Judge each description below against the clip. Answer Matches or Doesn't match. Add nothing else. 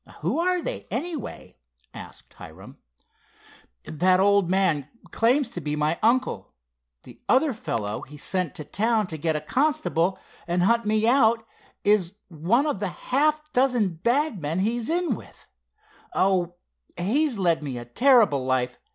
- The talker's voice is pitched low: Doesn't match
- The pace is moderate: Matches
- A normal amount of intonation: Doesn't match